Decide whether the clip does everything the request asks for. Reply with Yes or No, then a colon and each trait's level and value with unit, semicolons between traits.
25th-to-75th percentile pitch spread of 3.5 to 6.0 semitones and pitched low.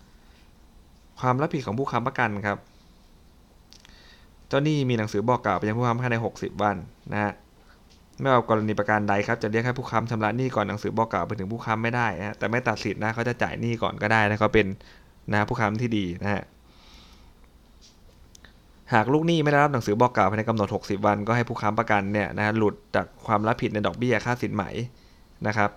No: narrow, 2.6 semitones; low, 105 Hz